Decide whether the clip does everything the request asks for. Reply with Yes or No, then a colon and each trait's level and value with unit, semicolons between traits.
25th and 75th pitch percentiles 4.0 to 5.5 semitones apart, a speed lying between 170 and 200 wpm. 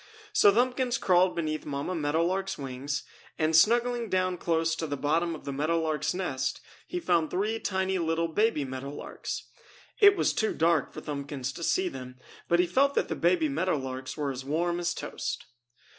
Yes: average, 4.4 semitones; average, 190 wpm